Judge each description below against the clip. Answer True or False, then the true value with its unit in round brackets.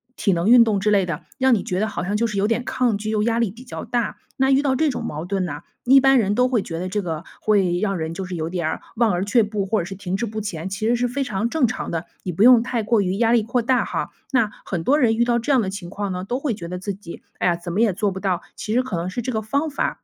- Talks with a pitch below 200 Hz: False (210 Hz)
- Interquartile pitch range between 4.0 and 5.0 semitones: True (4.5 semitones)